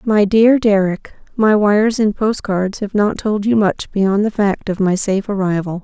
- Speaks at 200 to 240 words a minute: Yes, fast, 205 wpm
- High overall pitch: Yes, high, 205 Hz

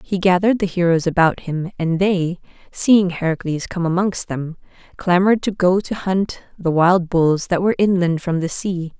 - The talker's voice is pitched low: No, medium, 180 Hz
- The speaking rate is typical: Yes, average, 180 wpm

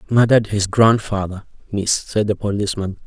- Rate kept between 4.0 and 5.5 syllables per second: Yes, 5.4 syllables/s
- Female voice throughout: No, male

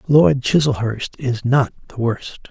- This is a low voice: Yes, low, 125 Hz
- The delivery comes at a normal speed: Yes, average, 145 wpm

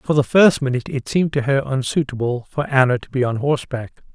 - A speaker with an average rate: No, fast, 215 wpm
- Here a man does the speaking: Yes, male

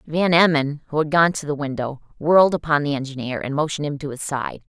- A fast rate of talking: Yes, fast, 225 wpm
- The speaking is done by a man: No, female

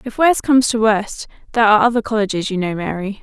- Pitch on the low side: No, high, 215 Hz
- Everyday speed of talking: No, fast, 225 wpm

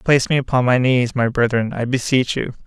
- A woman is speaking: No, male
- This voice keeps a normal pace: No, fast, 225 wpm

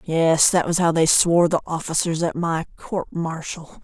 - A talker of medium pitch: Yes, medium, 165 Hz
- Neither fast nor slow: Yes, average, 190 wpm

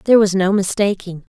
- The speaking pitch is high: Yes, high, 195 Hz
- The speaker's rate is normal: Yes, average, 180 wpm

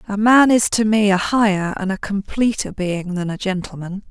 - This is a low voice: No, high, 200 Hz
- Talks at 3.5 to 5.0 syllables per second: Yes, 4.9 syllables/s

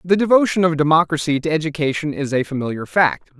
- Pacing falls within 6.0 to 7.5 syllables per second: Yes, 6.2 syllables/s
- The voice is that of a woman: No, male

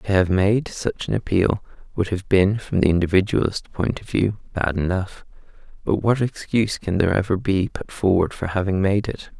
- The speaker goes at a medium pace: Yes, average, 190 wpm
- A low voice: Yes, very low, 95 Hz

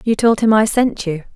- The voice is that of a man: No, female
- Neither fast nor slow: No, fast, 265 wpm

